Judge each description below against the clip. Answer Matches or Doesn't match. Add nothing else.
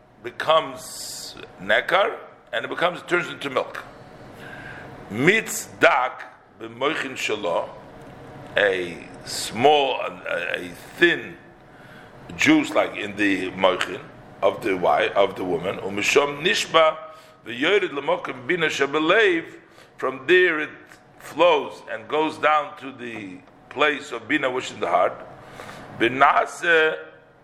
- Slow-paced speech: Matches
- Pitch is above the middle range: Doesn't match